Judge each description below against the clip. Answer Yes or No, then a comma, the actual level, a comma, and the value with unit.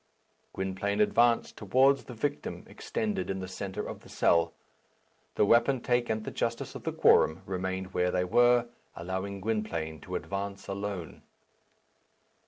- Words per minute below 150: Yes, average, 140 wpm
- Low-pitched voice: Yes, low, 100 Hz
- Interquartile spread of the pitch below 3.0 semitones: No, average, 4.2 semitones